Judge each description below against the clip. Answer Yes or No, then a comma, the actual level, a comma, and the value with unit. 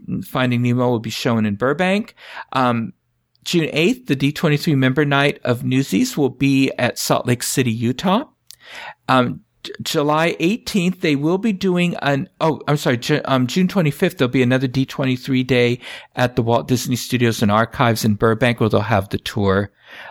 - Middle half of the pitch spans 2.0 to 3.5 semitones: No, average, 4.2 semitones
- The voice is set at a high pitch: No, low, 130 Hz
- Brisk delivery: No, average, 175 wpm